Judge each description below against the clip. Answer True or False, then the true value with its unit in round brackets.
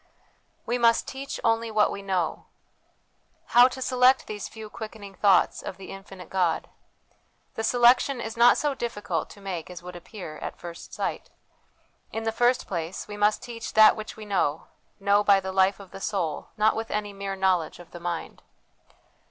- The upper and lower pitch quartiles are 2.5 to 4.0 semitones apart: True (3.2 semitones)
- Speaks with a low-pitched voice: False (205 Hz)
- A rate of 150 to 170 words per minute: False (180 wpm)